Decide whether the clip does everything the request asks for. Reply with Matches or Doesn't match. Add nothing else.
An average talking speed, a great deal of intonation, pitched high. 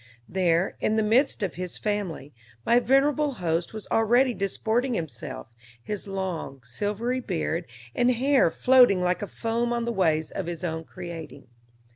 Matches